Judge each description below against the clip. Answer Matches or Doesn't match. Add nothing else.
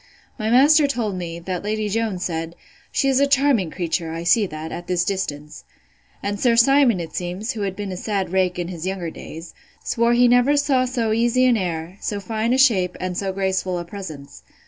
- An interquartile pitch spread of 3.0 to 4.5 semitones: Doesn't match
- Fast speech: Matches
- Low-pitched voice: Doesn't match